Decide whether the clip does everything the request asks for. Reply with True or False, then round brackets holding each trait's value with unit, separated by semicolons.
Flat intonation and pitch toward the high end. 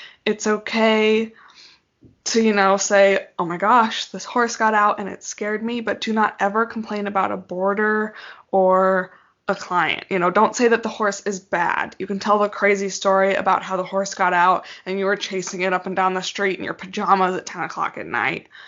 True (2.2 semitones; 200 Hz)